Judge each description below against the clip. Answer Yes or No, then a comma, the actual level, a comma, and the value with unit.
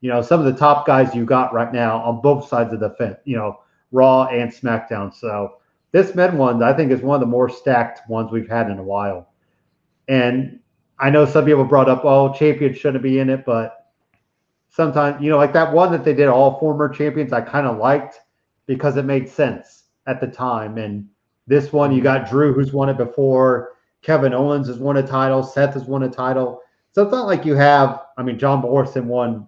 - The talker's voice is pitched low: Yes, low, 130 Hz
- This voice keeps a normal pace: No, fast, 220 wpm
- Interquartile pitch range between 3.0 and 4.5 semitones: Yes, average, 3.3 semitones